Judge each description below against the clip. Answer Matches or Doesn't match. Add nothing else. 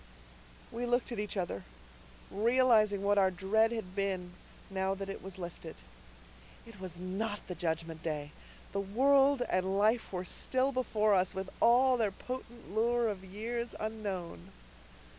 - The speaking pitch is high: Matches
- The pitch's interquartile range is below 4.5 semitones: Matches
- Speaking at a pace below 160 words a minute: Matches